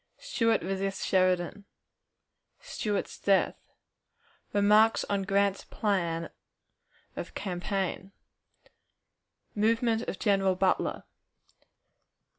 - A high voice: Yes, high, 195 Hz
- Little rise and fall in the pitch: Yes, narrow, 1.8 semitones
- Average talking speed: No, slow, 75 wpm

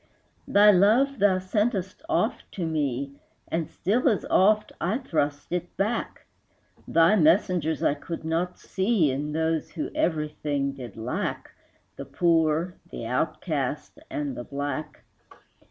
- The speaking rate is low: Yes, slow, 130 wpm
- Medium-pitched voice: Yes, medium, 165 Hz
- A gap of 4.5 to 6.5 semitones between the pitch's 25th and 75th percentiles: Yes, average, 5.1 semitones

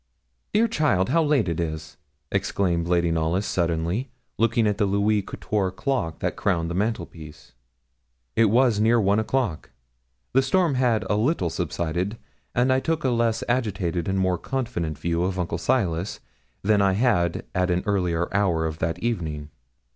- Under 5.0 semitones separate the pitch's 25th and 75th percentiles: No, wide, 5.5 semitones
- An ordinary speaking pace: Yes, average, 160 wpm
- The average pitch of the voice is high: No, very low, 95 Hz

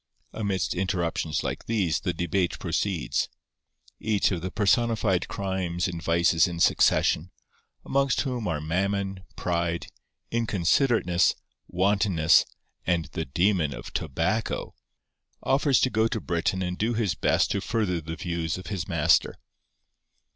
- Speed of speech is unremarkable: No, slow, 125 wpm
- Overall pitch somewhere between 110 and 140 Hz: No, very low, 90 Hz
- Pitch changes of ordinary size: Yes, average, 3.6 semitones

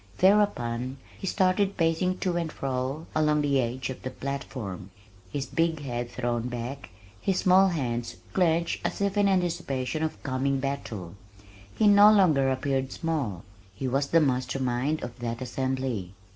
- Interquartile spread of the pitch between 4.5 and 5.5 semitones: Yes, average, 5.1 semitones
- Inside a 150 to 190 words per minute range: Yes, average, 155 wpm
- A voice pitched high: No, low, 135 Hz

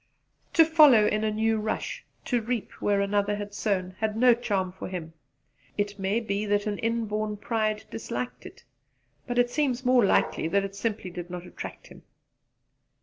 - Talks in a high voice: Yes, high, 210 Hz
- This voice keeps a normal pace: Yes, average, 175 wpm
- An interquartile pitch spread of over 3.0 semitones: No, average, 2.7 semitones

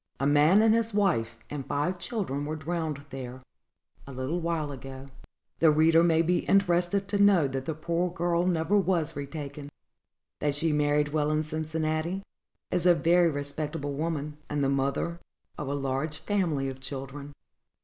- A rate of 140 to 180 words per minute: Yes, average, 165 wpm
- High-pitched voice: No, medium, 155 Hz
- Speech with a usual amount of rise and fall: Yes, average, 3.4 semitones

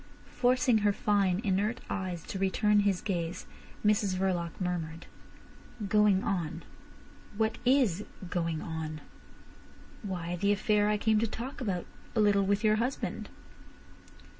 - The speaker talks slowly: Yes, slow, 130 wpm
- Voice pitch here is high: Yes, high, 200 Hz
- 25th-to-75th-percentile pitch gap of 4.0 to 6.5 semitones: No, average, 3.1 semitones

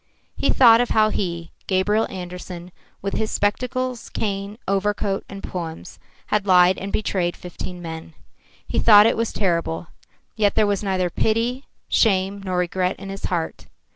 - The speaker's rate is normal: Yes, average, 155 wpm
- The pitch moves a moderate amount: Yes, average, 3.0 semitones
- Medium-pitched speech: No, high, 195 Hz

